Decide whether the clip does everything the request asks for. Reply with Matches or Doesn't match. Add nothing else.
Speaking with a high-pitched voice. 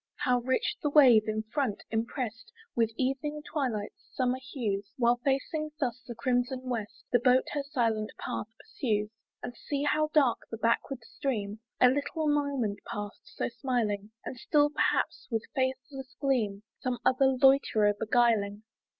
Matches